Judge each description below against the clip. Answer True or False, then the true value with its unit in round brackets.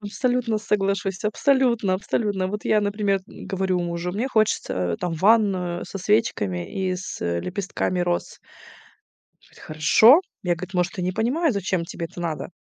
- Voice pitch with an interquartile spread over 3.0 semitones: True (3.5 semitones)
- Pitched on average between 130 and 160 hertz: False (195 Hz)